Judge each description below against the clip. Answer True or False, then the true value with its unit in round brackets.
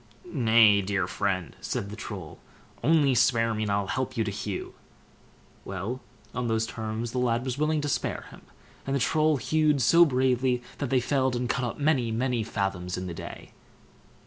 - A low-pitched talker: True (120 Hz)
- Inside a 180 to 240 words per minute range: True (185 wpm)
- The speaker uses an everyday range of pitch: True (4.1 semitones)